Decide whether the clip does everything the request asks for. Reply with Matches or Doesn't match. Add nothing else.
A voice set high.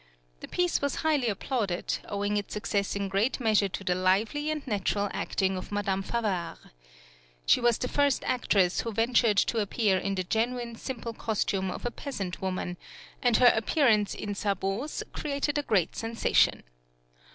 Matches